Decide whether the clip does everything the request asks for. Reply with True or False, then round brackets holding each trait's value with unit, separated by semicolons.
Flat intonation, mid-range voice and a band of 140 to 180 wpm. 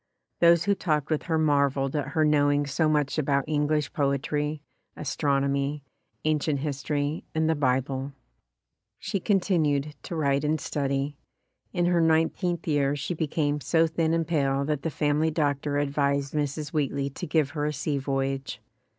True (2.1 semitones; 145 Hz; 160 wpm)